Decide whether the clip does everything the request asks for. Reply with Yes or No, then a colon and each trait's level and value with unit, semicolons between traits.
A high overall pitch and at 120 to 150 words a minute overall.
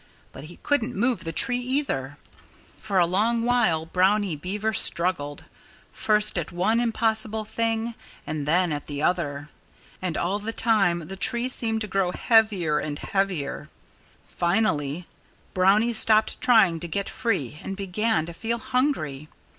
Yes: high, 195 Hz; average, 145 wpm